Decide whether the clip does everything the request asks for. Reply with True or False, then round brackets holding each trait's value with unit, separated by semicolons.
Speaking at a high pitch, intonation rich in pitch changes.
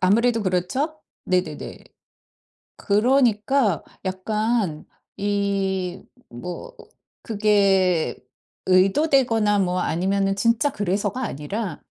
False (200 Hz; 3.6 semitones)